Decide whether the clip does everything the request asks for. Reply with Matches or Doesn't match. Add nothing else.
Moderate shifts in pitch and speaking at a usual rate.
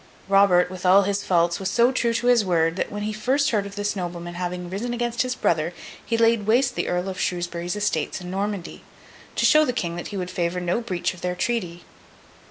Doesn't match